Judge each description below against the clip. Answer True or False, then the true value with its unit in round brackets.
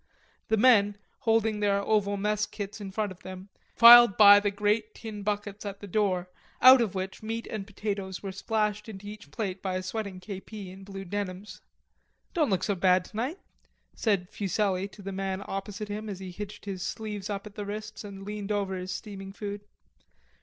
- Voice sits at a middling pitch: False (205 Hz)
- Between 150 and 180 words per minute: False (190 wpm)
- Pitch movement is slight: True (1.7 semitones)